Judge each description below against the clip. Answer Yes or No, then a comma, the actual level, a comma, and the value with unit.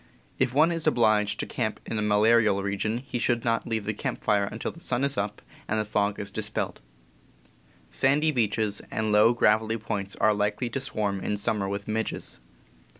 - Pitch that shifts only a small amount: Yes, narrow, 2.2 semitones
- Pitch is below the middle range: Yes, low, 110 Hz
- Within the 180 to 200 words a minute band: Yes, average, 185 wpm